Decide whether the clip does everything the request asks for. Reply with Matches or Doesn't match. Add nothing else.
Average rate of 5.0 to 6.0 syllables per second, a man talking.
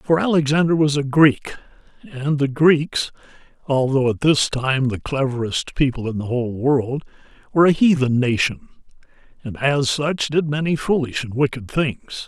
Doesn't match